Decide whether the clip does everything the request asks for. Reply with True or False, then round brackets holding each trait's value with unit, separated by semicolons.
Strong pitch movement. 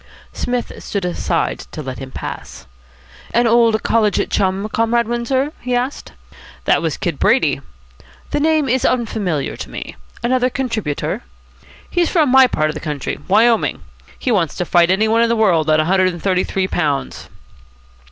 True (5.7 semitones)